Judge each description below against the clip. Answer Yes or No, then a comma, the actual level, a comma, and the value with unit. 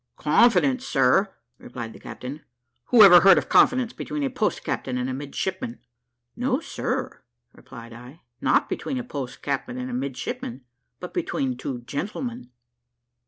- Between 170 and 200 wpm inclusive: No, average, 150 wpm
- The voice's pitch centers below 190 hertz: Yes, medium, 140 Hz